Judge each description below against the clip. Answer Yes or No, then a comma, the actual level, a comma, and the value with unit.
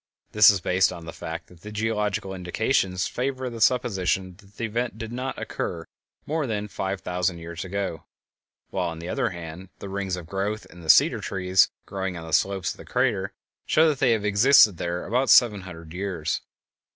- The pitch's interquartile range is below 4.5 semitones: Yes, average, 3.9 semitones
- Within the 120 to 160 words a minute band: No, average, 195 wpm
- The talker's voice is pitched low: Yes, very low, 95 Hz